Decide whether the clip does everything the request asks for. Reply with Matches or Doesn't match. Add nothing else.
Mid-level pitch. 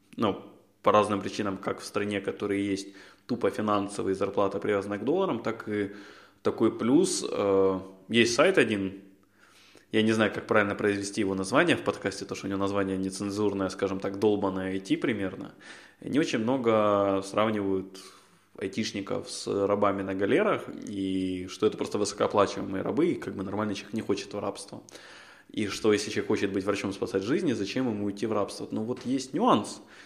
Doesn't match